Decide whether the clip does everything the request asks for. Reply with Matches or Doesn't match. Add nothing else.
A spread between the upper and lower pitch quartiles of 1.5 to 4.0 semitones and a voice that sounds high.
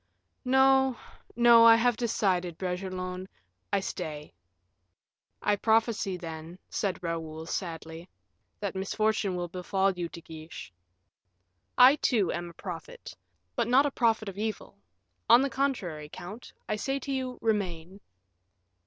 Doesn't match